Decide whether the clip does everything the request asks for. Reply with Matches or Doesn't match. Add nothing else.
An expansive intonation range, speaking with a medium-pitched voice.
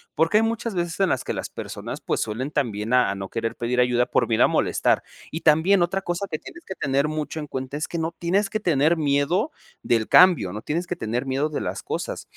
Matches